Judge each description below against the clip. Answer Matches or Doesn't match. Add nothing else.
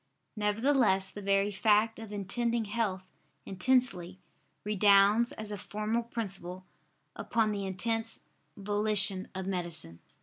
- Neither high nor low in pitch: Doesn't match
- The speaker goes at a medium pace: Doesn't match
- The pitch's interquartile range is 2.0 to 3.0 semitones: Matches